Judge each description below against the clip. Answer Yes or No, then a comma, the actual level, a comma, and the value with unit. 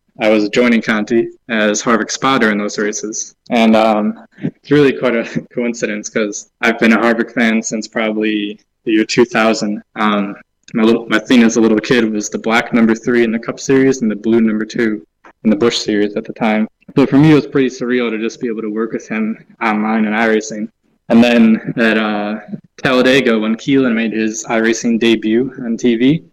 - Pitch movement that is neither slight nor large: No, narrow, 2.1 semitones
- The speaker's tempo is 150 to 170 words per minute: No, average, 200 wpm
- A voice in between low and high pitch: No, low, 115 Hz